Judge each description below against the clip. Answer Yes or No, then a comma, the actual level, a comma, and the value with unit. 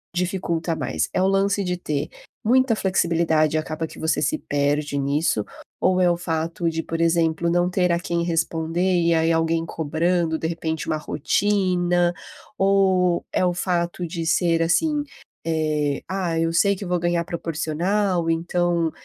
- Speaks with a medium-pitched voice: Yes, medium, 170 Hz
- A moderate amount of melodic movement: No, narrow, 1.9 semitones